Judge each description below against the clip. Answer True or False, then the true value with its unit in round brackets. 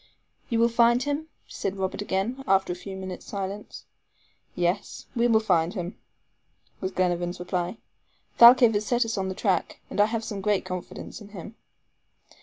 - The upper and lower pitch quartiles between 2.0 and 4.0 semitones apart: True (3.7 semitones)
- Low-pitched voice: False (200 Hz)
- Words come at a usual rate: True (160 wpm)